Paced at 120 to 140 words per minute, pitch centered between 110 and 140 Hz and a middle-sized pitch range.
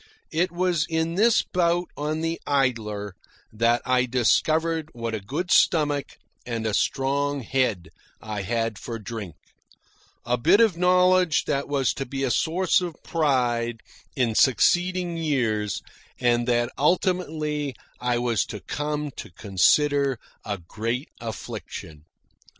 No: slow, 135 wpm; low, 135 Hz; wide, 5.8 semitones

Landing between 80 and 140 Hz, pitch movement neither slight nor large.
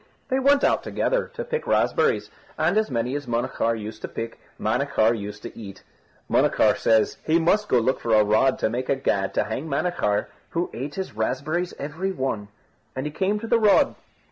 No: low, 135 Hz; wide, 8.1 semitones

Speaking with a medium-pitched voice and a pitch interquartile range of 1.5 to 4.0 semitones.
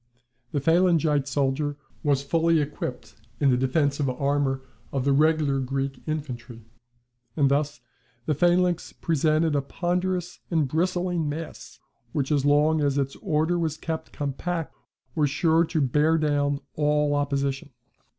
Yes: medium, 145 Hz; average, 2.7 semitones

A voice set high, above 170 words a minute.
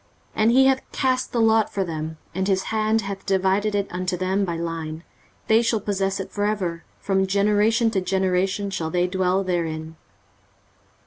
Yes: high, 195 Hz; average, 180 wpm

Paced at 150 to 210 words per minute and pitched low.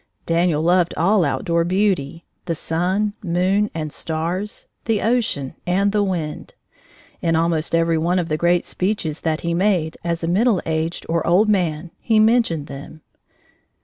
No: average, 155 wpm; medium, 170 Hz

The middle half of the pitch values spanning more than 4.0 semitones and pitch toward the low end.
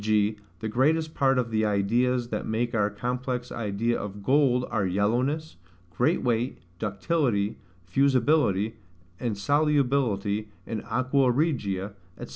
Yes: average, 4.4 semitones; low, 120 Hz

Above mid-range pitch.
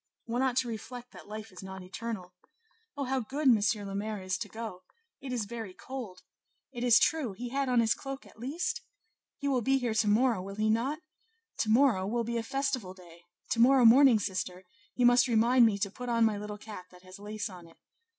Yes: high, 225 Hz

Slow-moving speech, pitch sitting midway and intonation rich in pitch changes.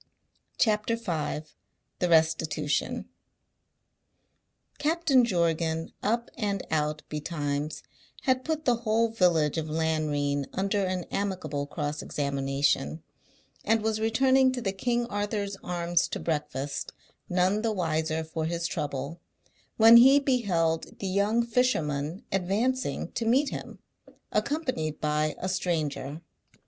Yes: slow, 115 wpm; medium, 180 Hz; wide, 6.6 semitones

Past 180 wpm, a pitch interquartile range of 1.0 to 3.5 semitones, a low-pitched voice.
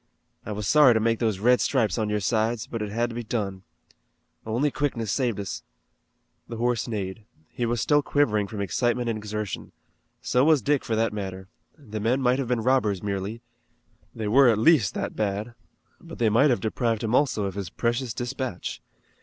Yes: average, 195 wpm; average, 2.9 semitones; low, 115 Hz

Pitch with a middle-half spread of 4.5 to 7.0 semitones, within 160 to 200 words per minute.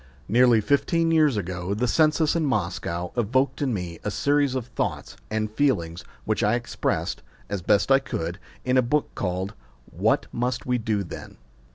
Yes: wide, 5.6 semitones; average, 170 wpm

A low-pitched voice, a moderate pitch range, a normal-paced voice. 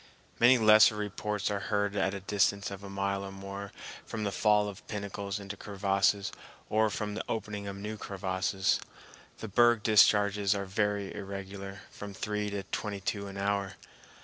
No: low, 100 Hz; narrow, 1.1 semitones; average, 170 wpm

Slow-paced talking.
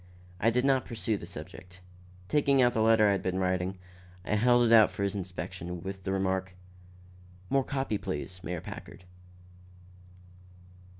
No: average, 160 wpm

